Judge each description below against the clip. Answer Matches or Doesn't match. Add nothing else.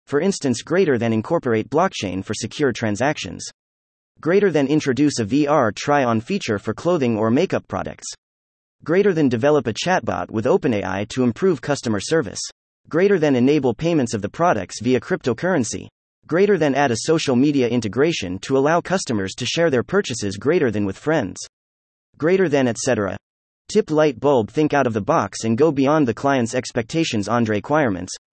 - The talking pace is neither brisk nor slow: Matches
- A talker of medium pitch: Doesn't match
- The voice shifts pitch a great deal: Matches